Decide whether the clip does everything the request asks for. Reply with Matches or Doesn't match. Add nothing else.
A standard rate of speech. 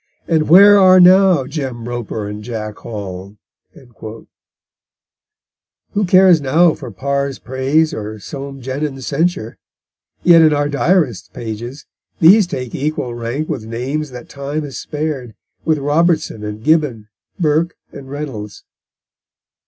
Doesn't match